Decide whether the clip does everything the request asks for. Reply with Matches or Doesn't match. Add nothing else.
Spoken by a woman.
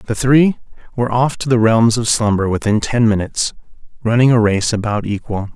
Doesn't match